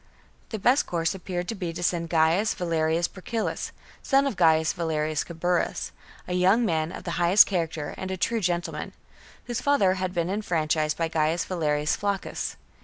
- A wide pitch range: No, average, 3.0 semitones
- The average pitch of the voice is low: No, medium, 175 Hz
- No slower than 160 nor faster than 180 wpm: Yes, average, 170 wpm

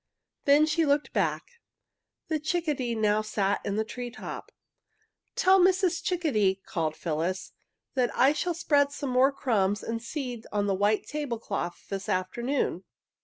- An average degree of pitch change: No, wide, 6.6 semitones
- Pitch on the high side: Yes, high, 245 Hz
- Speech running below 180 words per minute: Yes, average, 150 wpm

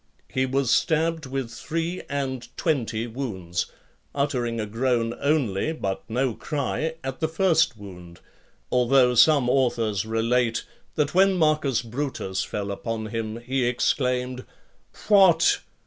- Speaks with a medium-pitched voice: No, low, 125 Hz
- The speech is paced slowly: Yes, slow, 125 wpm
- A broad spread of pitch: No, average, 4.4 semitones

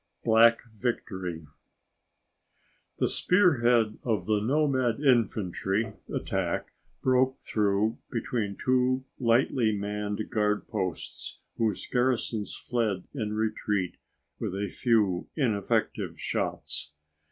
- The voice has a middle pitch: No, low, 110 Hz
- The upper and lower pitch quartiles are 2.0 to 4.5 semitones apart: Yes, average, 3.2 semitones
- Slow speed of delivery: Yes, slow, 95 wpm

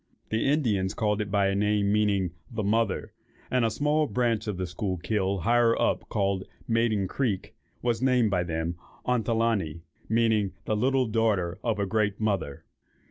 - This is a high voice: No, low, 105 Hz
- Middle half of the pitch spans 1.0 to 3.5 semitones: Yes, average, 2.9 semitones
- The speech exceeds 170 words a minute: No, average, 160 wpm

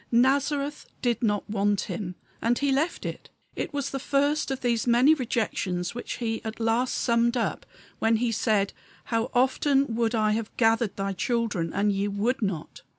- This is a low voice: No, high, 230 Hz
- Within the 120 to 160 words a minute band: No, average, 175 wpm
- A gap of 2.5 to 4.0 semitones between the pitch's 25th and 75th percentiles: Yes, average, 3.6 semitones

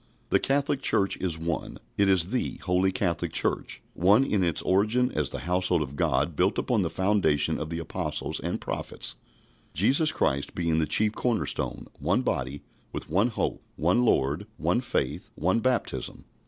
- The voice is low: Yes, very low, 95 Hz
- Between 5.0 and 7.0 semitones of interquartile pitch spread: Yes, wide, 5.5 semitones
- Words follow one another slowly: No, average, 170 wpm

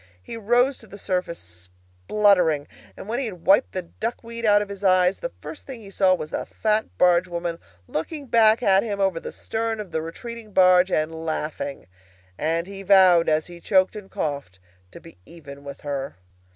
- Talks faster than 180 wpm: Yes, average, 195 wpm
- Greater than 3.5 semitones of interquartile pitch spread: Yes, average, 4.5 semitones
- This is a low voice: No, medium, 185 Hz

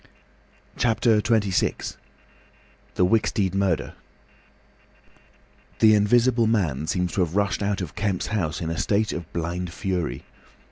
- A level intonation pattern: No, average, 3.6 semitones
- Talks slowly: Yes, slow, 125 wpm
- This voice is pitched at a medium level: No, low, 100 Hz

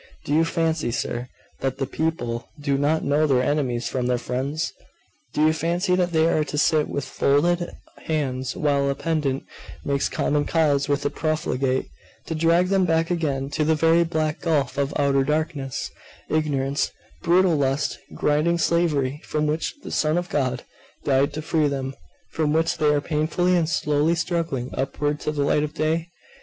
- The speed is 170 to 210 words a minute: Yes, average, 175 wpm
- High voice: No, medium, 150 Hz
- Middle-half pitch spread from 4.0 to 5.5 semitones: No, average, 2.8 semitones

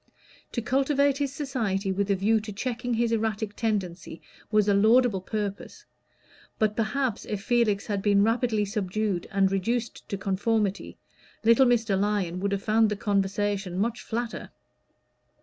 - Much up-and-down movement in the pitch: No, average, 2.7 semitones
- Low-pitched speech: No, high, 215 Hz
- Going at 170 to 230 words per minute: No, average, 150 wpm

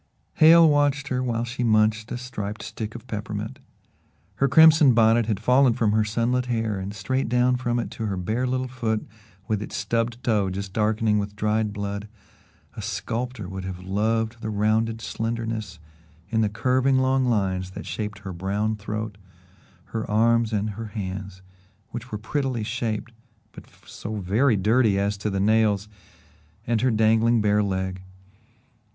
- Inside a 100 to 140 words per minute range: No, average, 165 wpm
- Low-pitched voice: Yes, low, 110 Hz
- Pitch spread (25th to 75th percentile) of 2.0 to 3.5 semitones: Yes, average, 2.7 semitones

